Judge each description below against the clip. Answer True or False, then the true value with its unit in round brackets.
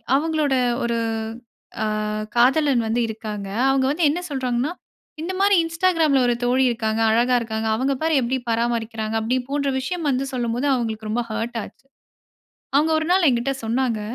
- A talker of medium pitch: False (250 Hz)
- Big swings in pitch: False (4.1 semitones)